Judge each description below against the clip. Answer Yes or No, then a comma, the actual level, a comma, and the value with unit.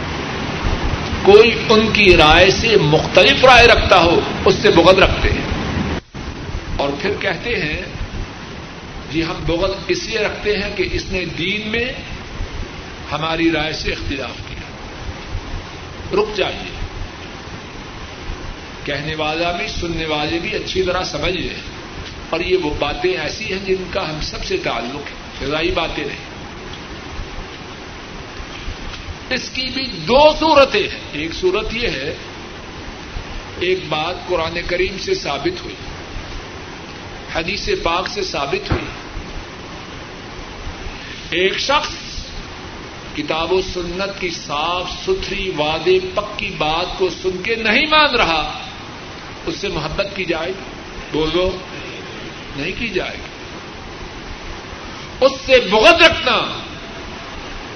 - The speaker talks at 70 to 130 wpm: Yes, average, 120 wpm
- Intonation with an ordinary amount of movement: No, wide, 5.8 semitones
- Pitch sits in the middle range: Yes, medium, 180 Hz